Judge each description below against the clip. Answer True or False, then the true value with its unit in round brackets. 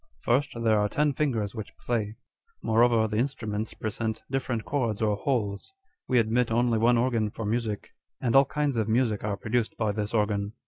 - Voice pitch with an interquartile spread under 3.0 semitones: True (2.5 semitones)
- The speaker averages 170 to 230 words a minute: True (180 wpm)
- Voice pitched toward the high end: False (115 Hz)